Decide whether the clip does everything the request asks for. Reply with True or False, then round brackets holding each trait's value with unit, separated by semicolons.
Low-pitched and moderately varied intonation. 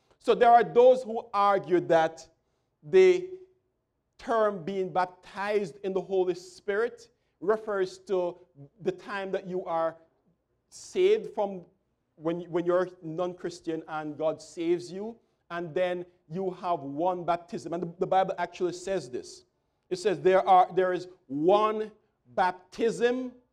False (185 Hz; 3.6 semitones)